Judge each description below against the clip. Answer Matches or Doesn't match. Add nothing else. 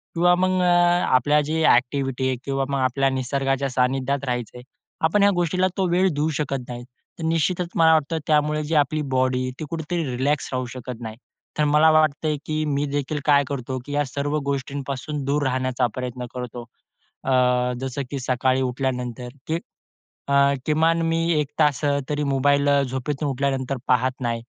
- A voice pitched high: Doesn't match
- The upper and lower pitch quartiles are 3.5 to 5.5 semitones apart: Doesn't match